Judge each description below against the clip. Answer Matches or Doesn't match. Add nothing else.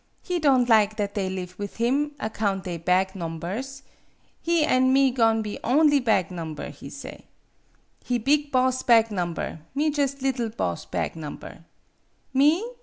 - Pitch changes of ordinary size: Doesn't match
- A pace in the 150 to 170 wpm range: Matches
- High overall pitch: Matches